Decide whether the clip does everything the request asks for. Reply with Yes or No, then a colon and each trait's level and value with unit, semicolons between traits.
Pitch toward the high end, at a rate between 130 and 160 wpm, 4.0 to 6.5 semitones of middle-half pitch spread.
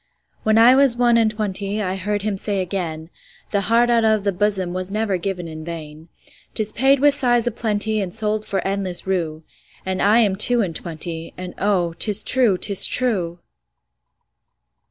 No: high, 200 Hz; average, 155 wpm; average, 3.5 semitones